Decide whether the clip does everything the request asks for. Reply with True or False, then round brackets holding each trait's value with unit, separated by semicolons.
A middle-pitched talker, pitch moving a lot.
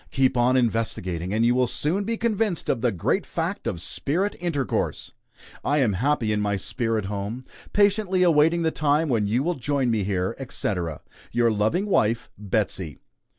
False (120 Hz; 7.2 semitones)